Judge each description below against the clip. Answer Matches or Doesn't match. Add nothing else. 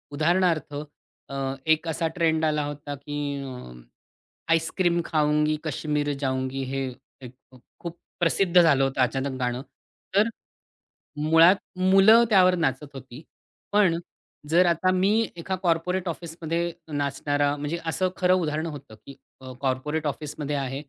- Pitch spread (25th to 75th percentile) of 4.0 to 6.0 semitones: Doesn't match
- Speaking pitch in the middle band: Matches